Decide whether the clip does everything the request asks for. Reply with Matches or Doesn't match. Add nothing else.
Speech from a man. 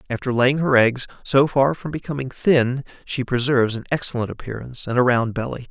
Matches